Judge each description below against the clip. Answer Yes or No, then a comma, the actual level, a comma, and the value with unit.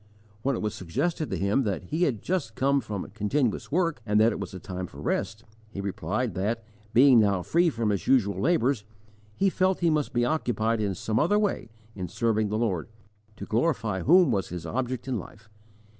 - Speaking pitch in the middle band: No, low, 115 Hz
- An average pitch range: No, wide, 5.7 semitones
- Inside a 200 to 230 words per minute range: Yes, fast, 205 wpm